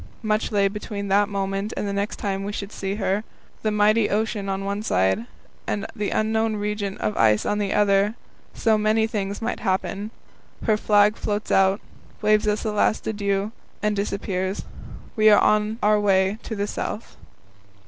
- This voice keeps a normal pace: Yes, average, 175 wpm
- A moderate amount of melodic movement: No, narrow, 1.3 semitones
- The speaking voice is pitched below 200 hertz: No, high, 205 Hz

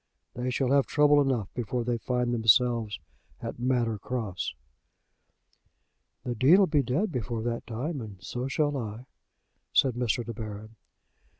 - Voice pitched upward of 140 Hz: No, low, 120 Hz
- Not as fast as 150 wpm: Yes, average, 140 wpm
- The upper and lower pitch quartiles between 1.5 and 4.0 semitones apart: Yes, average, 2.8 semitones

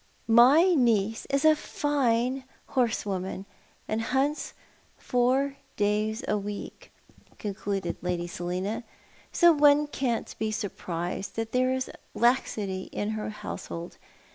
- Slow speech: Yes, slow, 115 wpm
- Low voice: No, high, 225 Hz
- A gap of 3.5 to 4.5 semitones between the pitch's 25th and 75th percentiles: No, average, 4.9 semitones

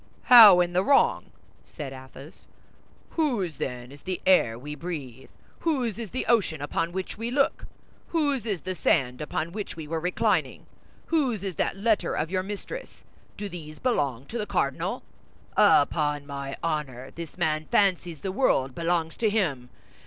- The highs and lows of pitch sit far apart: Yes, wide, 6.1 semitones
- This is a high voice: No, medium, 175 Hz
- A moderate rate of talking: Yes, average, 160 wpm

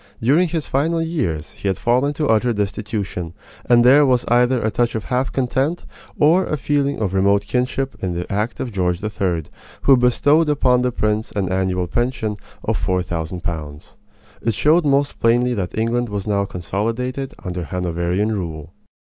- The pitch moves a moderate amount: No, wide, 5.7 semitones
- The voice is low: Yes, low, 110 Hz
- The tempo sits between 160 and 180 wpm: Yes, average, 175 wpm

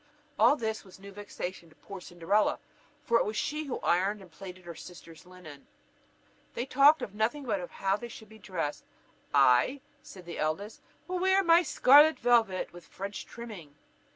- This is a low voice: No, high, 205 Hz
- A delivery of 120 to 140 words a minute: No, average, 175 wpm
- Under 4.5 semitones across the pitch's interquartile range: No, wide, 5.4 semitones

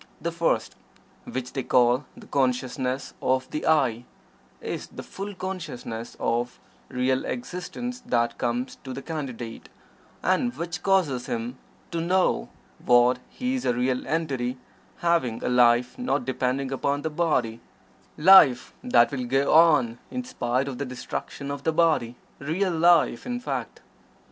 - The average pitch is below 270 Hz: Yes, low, 135 Hz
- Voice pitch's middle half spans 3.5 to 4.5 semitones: No, wide, 5.4 semitones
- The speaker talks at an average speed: Yes, average, 145 wpm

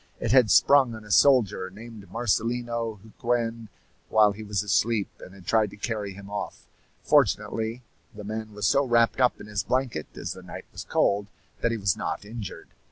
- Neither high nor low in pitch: No, low, 110 Hz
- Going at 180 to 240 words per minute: Yes, average, 185 wpm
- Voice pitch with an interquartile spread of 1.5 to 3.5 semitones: Yes, narrow, 2.4 semitones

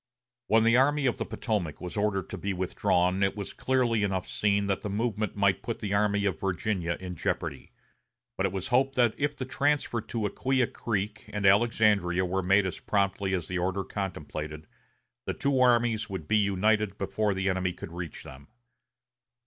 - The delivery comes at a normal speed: Yes, average, 185 wpm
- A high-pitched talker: No, low, 100 Hz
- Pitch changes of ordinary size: Yes, average, 3.2 semitones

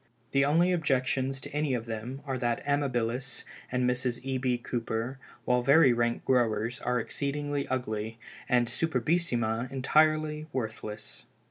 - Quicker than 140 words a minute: No, slow, 135 wpm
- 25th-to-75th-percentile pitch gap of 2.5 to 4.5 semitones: Yes, average, 3.0 semitones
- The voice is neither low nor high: No, low, 130 Hz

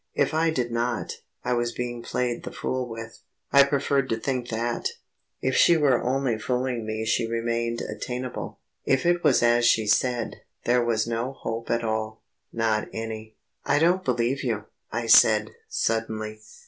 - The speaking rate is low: No, average, 165 wpm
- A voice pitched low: Yes, low, 120 Hz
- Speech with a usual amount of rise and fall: No, narrow, 2.2 semitones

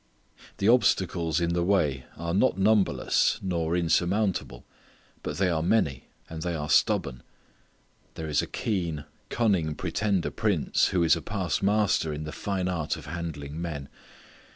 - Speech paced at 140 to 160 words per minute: Yes, average, 150 wpm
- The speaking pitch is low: Yes, very low, 85 Hz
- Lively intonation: No, average, 3.6 semitones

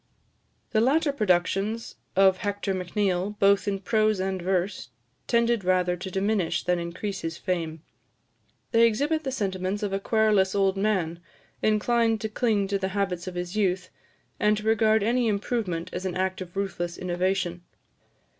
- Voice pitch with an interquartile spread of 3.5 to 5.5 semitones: No, average, 2.9 semitones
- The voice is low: No, high, 195 Hz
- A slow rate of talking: No, average, 155 wpm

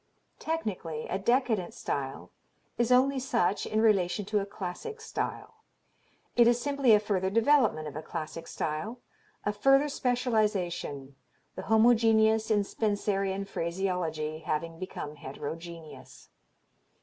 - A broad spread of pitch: Yes, wide, 5.9 semitones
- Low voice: No, high, 200 Hz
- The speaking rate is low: Yes, slow, 120 wpm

